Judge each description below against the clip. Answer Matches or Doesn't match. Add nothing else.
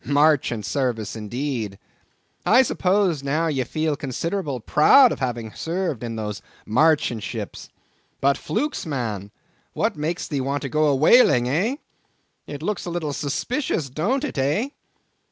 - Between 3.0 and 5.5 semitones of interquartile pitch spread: Matches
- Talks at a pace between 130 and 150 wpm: Matches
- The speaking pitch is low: Doesn't match